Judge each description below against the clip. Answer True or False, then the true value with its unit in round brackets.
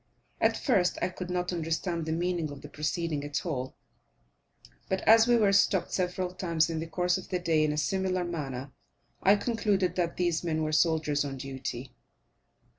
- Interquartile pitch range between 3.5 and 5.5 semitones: False (3.0 semitones)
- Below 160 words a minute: False (185 wpm)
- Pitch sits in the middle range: True (170 Hz)